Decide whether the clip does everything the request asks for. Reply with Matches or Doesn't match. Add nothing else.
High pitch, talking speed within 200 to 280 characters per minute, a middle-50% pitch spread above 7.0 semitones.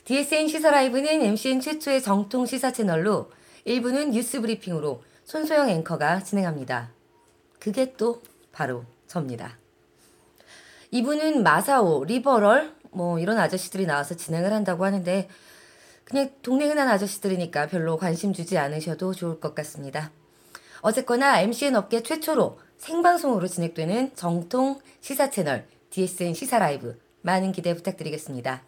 Doesn't match